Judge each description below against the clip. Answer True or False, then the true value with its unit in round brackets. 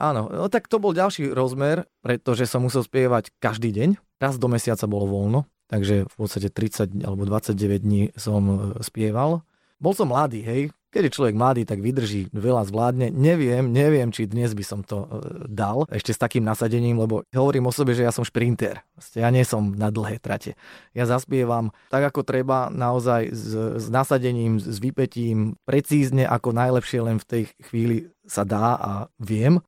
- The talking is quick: True (175 wpm)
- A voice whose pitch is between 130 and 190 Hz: False (120 Hz)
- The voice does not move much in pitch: False (3.7 semitones)